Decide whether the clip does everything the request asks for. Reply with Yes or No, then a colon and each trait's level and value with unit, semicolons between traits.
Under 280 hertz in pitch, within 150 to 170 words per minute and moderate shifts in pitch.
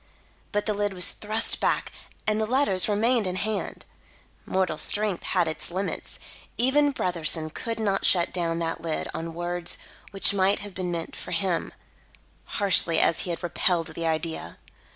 Yes: medium, 185 Hz; average, 165 wpm; average, 3.7 semitones